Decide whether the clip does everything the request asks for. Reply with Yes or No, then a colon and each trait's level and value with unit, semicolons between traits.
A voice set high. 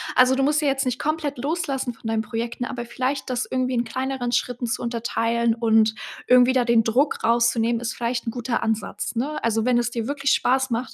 Yes: high, 245 Hz